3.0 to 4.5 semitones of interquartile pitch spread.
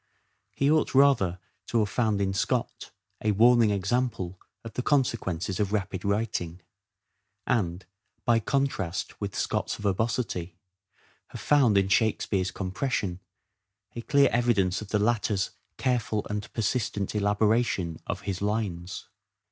Yes: average, 3.7 semitones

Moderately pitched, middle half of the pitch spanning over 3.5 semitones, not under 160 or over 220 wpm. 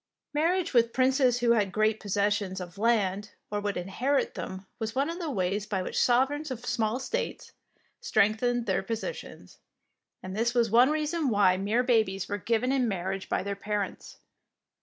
No: high, 225 Hz; average, 4.4 semitones; average, 175 wpm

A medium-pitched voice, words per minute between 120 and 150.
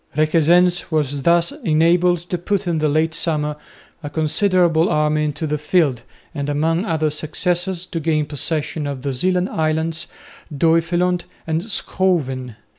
Yes: medium, 160 Hz; average, 140 wpm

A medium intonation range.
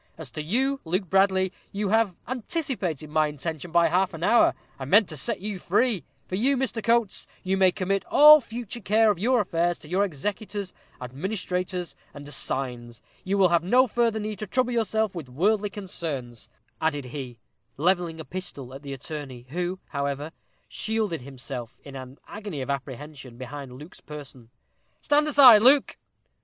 No: wide, 6.8 semitones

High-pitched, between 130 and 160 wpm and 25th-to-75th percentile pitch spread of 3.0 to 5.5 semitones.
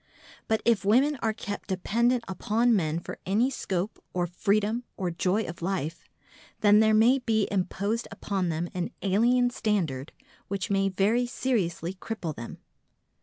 Yes: high, 205 Hz; average, 150 wpm; average, 4.0 semitones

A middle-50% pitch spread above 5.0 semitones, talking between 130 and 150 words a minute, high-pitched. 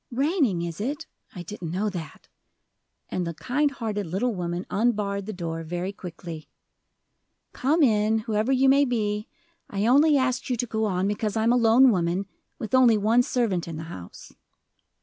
No: wide, 5.5 semitones; average, 175 wpm; high, 215 Hz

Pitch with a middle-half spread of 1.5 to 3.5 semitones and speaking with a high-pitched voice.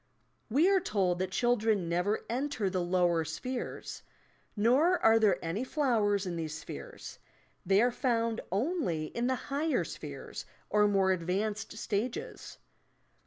No: average, 5.1 semitones; high, 210 Hz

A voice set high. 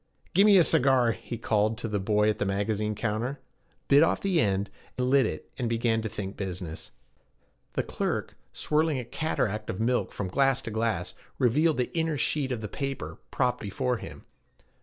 No: low, 115 Hz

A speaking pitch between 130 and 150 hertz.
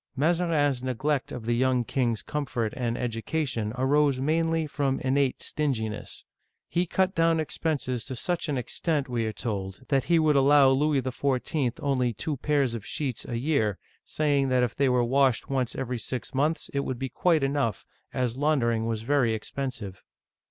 Yes: low, 135 Hz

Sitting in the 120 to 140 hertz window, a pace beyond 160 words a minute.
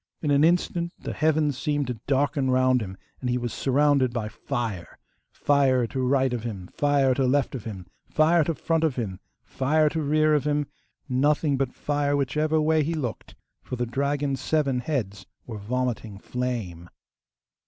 Yes: low, 135 Hz; average, 175 wpm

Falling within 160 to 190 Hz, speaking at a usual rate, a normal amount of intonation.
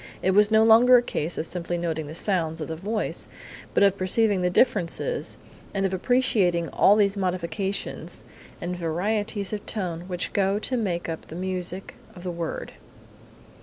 Yes: medium, 185 Hz; average, 170 wpm; average, 3.3 semitones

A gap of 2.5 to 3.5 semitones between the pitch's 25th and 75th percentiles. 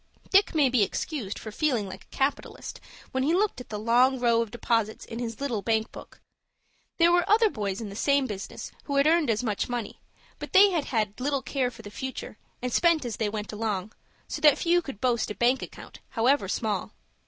No: average, 4.7 semitones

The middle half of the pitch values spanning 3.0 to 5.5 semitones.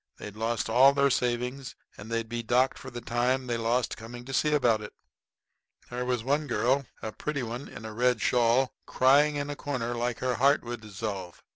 No: narrow, 2.4 semitones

